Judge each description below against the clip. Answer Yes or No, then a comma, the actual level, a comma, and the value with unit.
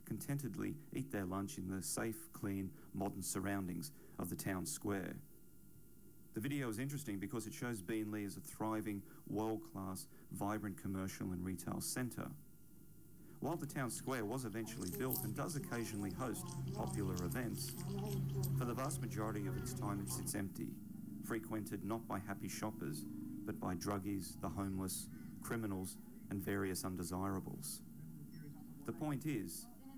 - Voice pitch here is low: Yes, low, 105 Hz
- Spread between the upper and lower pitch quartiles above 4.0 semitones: Yes, average, 4.8 semitones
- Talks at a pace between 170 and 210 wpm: No, average, 145 wpm